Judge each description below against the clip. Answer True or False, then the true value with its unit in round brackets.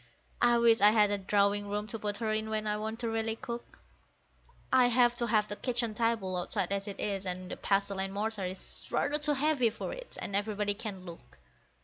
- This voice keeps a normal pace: False (220 wpm)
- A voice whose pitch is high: True (210 Hz)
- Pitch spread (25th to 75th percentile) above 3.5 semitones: False (2.6 semitones)